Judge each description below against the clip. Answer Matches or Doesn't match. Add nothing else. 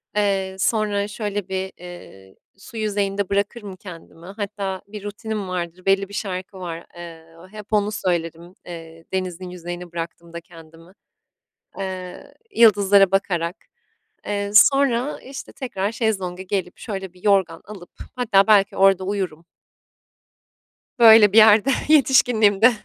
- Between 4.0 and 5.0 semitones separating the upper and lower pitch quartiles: Doesn't match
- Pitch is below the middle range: Doesn't match